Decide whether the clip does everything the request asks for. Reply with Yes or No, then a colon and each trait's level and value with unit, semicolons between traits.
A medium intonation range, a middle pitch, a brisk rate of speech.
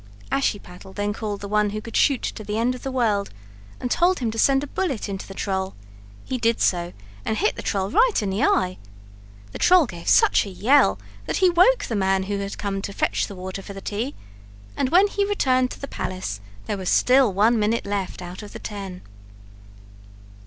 No: average, 4.9 semitones; high, 210 Hz; fast, 215 wpm